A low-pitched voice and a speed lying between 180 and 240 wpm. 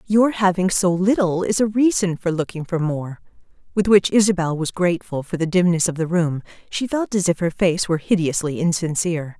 No: medium, 180 Hz; average, 200 wpm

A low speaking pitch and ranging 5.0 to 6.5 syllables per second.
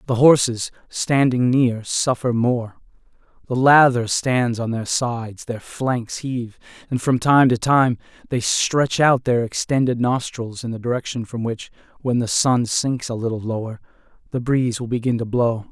No: low, 120 Hz; 4.5 syllables/s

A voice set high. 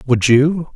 No: medium, 140 Hz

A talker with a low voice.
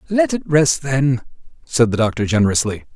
Yes: low, 125 Hz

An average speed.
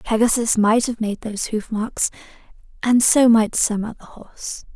Yes: average, 165 wpm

